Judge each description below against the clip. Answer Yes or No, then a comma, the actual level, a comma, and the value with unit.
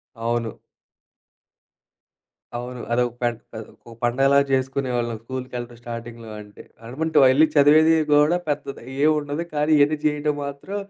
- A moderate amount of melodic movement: Yes, average, 3.7 semitones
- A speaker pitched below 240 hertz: Yes, low, 135 Hz